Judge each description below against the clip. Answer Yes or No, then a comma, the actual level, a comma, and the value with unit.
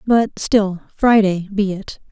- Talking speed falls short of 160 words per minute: Yes, average, 140 wpm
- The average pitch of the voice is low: No, high, 200 Hz